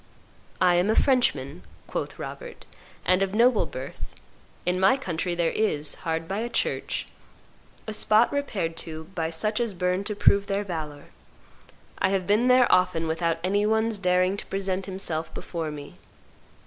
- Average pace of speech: Yes, average, 160 wpm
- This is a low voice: No, medium, 185 Hz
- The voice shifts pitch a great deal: No, average, 4.3 semitones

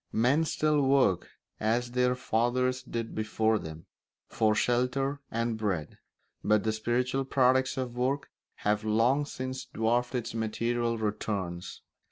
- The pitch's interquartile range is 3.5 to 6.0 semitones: No, average, 2.7 semitones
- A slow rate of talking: Yes, slow, 130 wpm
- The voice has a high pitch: No, low, 120 Hz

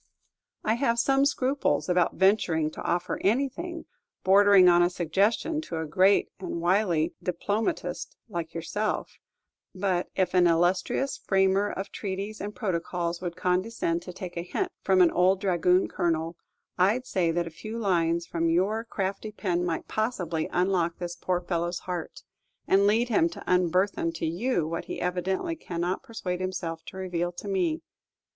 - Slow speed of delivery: No, average, 160 wpm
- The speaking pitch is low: No, medium, 185 Hz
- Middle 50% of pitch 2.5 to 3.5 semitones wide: Yes, average, 3.2 semitones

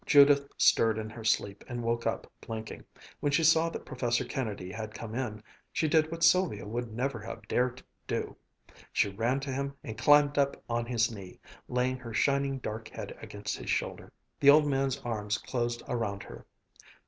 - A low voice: Yes, low, 120 Hz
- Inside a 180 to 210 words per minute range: Yes, average, 185 wpm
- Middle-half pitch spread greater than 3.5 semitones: Yes, average, 4.0 semitones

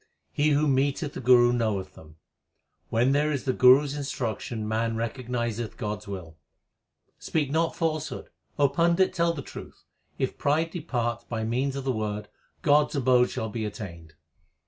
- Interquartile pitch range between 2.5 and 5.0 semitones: Yes, average, 4.6 semitones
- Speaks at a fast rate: No, average, 170 wpm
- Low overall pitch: Yes, low, 125 Hz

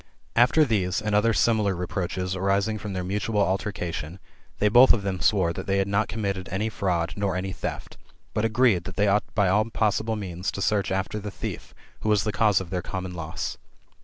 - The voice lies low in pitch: Yes, low, 100 Hz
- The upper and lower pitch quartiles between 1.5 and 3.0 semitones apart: Yes, narrow, 2.5 semitones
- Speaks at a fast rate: Yes, fast, 215 wpm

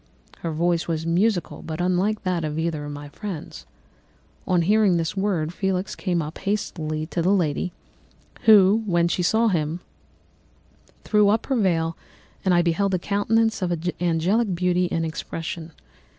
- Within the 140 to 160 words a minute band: Yes, average, 155 wpm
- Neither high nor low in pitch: Yes, medium, 175 Hz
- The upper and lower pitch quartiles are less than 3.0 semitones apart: No, average, 3.4 semitones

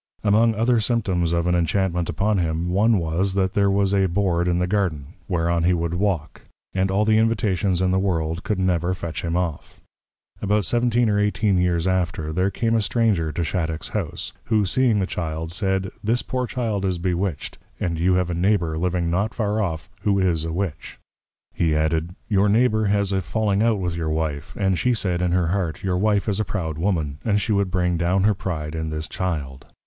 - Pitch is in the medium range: No, very low, 95 Hz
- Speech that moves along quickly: Yes, fast, 210 wpm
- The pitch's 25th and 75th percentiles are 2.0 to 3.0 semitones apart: No, average, 3.4 semitones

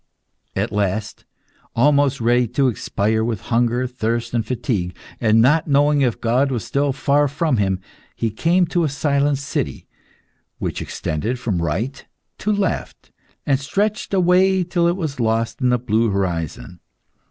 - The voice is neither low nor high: No, low, 125 Hz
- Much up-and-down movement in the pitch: No, average, 4.6 semitones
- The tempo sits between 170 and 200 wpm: No, average, 155 wpm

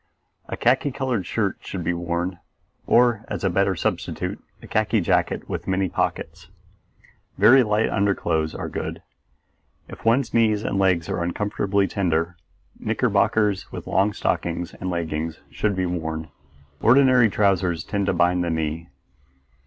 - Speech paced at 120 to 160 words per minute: Yes, average, 145 wpm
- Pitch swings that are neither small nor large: Yes, average, 3.8 semitones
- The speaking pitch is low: Yes, very low, 95 Hz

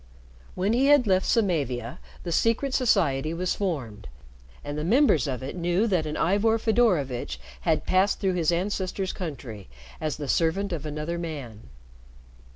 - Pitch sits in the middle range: Yes, medium, 170 Hz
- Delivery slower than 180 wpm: Yes, average, 155 wpm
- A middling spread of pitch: No, wide, 5.7 semitones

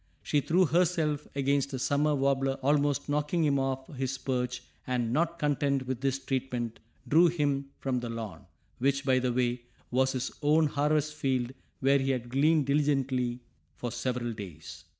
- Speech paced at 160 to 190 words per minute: Yes, average, 165 wpm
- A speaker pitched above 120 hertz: Yes, low, 135 Hz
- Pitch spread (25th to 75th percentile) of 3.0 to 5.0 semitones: No, narrow, 2.6 semitones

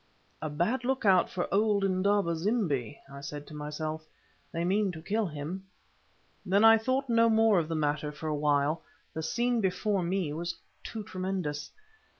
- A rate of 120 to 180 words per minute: Yes, average, 170 wpm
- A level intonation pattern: No, wide, 5.4 semitones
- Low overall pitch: No, medium, 180 Hz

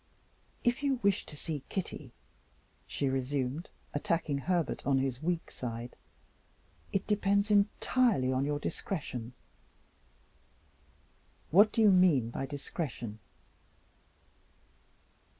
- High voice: No, medium, 150 Hz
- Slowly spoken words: Yes, slow, 100 wpm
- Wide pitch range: Yes, wide, 6.9 semitones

